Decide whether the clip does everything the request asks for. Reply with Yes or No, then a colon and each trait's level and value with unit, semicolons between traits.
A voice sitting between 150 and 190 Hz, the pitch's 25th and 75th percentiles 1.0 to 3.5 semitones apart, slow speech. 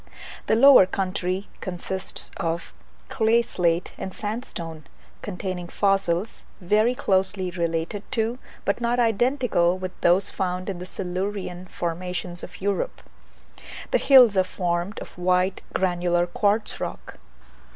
Yes: medium, 185 Hz; average, 2.9 semitones; slow, 120 wpm